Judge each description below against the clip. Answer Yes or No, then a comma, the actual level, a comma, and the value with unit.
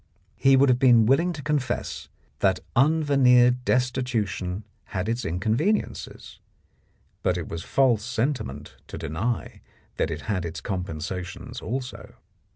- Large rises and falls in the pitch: Yes, wide, 6.4 semitones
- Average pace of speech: No, slow, 130 wpm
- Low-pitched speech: Yes, low, 120 Hz